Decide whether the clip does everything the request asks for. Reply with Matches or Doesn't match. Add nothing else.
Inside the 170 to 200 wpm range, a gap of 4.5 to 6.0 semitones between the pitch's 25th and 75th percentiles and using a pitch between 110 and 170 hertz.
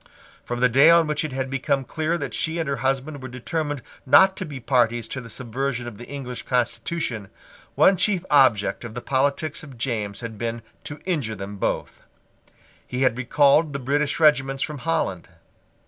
Doesn't match